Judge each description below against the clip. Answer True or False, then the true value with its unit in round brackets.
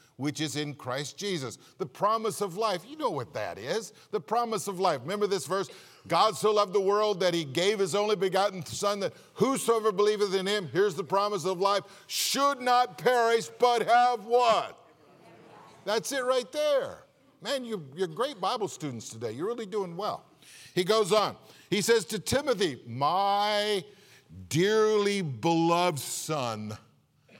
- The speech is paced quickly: False (165 wpm)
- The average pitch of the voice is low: False (205 Hz)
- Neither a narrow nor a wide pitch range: True (3.8 semitones)